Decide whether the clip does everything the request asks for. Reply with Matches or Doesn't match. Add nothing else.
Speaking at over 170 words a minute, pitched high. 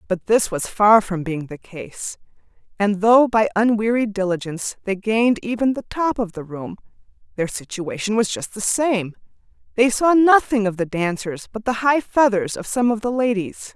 Matches